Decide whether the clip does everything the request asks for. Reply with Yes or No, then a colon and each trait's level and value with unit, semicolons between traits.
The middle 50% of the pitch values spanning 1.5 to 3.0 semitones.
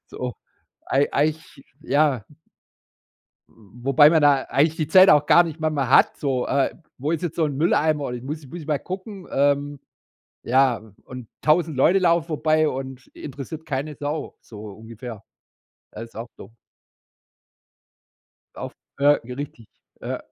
No: average, 3.4 semitones